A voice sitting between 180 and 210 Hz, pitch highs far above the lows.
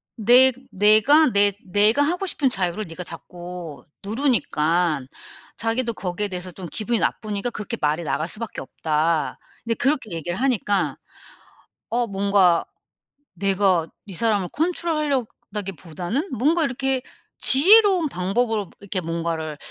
Yes: high, 205 Hz; wide, 6.1 semitones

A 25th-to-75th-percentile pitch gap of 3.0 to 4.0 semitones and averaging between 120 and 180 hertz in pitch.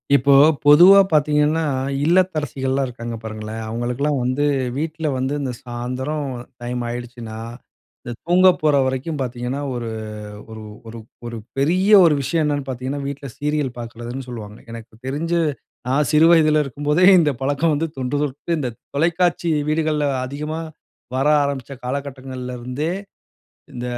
Yes: average, 3.6 semitones; medium, 140 Hz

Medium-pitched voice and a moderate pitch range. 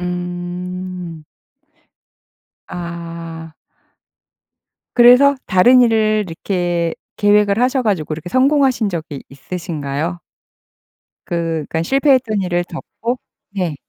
Yes: medium, 180 Hz; average, 4.7 semitones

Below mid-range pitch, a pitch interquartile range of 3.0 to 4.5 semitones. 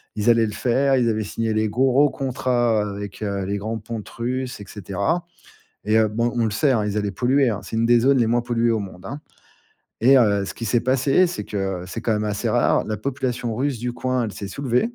Yes: low, 115 Hz; average, 3.4 semitones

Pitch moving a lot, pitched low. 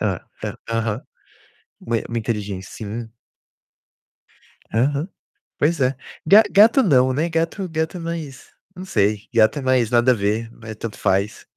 Yes: wide, 6.6 semitones; low, 125 Hz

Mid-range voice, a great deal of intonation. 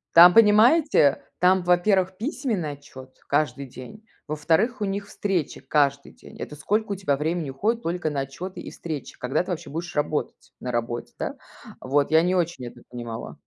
Yes: medium, 165 Hz; wide, 5.7 semitones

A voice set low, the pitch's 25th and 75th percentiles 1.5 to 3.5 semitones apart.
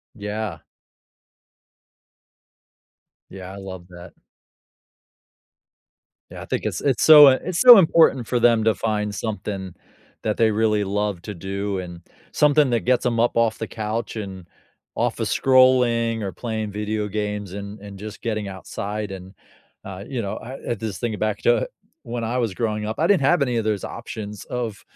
Yes: low, 110 Hz; average, 2.8 semitones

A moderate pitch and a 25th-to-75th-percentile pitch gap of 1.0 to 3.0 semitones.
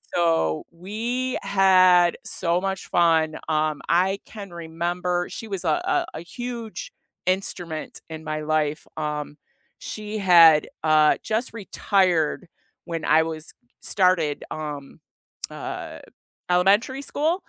No: medium, 175 Hz; average, 3.8 semitones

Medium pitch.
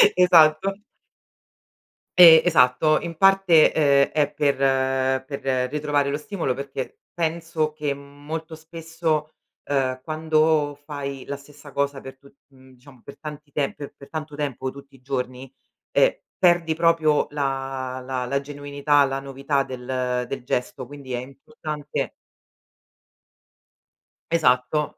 Yes: medium, 145 Hz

